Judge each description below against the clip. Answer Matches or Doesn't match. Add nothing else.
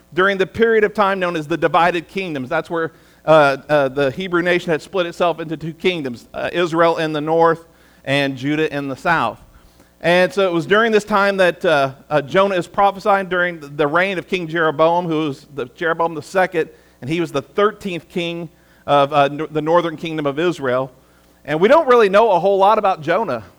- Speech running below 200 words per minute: Doesn't match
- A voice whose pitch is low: Doesn't match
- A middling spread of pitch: Matches